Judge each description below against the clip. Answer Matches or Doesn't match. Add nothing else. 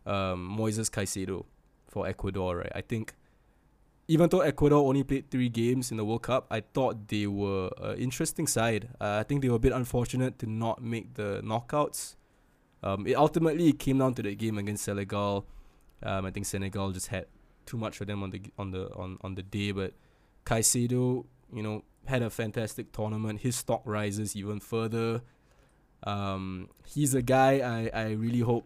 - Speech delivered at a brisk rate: Doesn't match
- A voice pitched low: Matches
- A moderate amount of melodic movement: Matches